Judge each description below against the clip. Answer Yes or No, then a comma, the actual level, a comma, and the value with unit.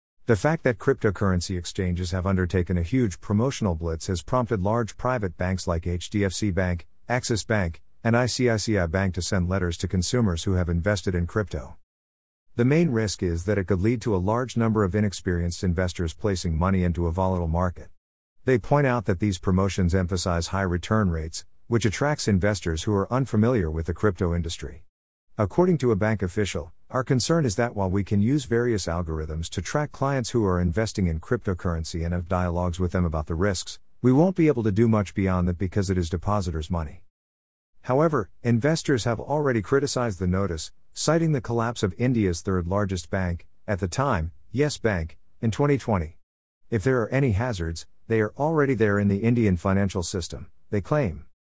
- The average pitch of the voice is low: Yes, very low, 95 Hz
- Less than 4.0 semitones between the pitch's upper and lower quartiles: No, average, 4.8 semitones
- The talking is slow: No, average, 185 wpm